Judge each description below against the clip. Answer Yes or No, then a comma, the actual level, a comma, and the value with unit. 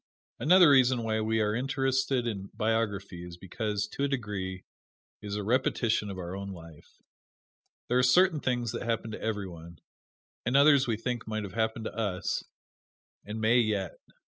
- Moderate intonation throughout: Yes, average, 3.9 semitones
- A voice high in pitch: No, low, 110 Hz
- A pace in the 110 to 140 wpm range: No, average, 175 wpm